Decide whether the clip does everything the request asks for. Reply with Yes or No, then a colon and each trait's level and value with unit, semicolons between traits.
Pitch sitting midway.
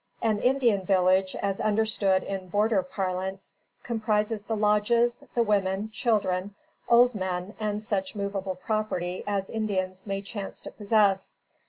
No: high, 205 Hz